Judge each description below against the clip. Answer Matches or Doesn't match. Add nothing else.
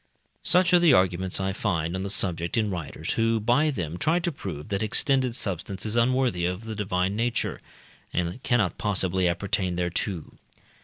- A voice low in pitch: Matches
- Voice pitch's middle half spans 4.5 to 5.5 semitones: Matches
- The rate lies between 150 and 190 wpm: Matches